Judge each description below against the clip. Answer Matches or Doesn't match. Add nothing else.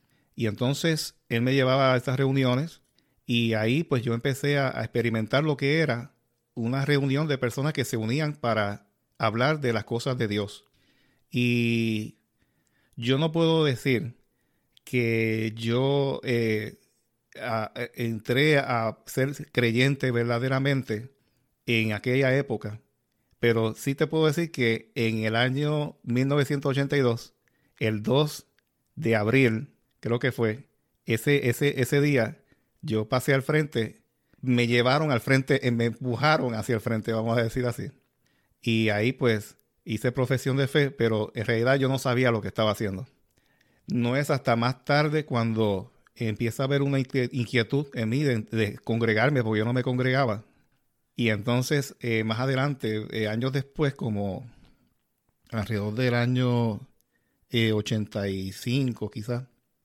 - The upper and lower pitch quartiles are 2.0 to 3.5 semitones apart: Matches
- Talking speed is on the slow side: Doesn't match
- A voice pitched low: Matches